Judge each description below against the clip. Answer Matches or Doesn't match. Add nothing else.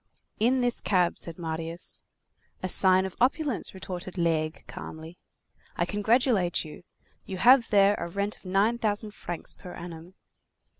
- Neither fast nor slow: Matches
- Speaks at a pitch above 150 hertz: Matches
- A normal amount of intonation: Matches